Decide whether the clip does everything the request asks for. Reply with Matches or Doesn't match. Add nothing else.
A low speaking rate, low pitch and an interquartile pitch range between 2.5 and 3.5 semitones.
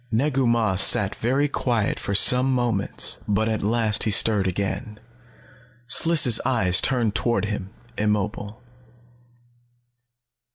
Matches